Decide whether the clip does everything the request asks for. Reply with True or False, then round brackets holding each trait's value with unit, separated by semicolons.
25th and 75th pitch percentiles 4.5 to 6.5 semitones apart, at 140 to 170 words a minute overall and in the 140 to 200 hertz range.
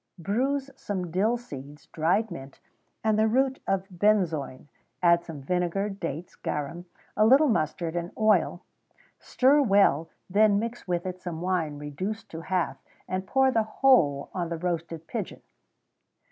True (4.8 semitones; 150 wpm; 185 Hz)